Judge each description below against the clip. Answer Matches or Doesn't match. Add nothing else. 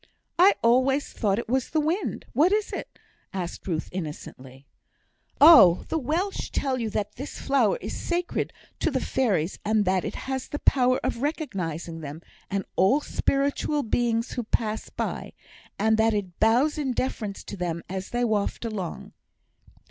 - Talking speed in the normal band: Matches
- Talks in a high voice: Matches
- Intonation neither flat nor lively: Doesn't match